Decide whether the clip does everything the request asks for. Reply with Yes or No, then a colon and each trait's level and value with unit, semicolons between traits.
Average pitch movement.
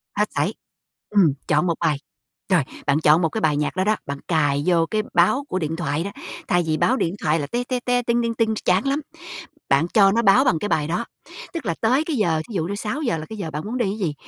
No: wide, 6.3 semitones